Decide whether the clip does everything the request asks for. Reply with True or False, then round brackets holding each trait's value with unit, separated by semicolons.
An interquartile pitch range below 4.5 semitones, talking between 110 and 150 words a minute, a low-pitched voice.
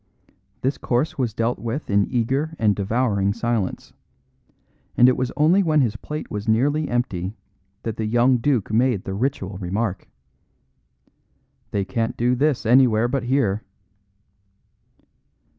True (3.9 semitones; 135 wpm; 120 Hz)